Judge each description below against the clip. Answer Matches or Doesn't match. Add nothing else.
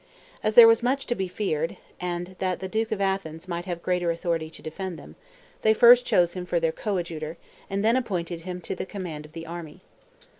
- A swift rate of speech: Matches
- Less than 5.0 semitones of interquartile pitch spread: Matches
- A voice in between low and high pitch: Matches